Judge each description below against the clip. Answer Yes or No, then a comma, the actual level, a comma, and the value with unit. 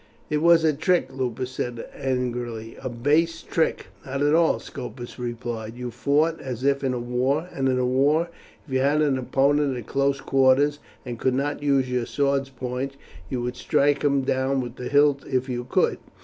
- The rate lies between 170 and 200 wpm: Yes, average, 185 wpm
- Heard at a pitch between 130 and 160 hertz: Yes, low, 135 Hz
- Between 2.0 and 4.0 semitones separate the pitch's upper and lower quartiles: Yes, narrow, 2.4 semitones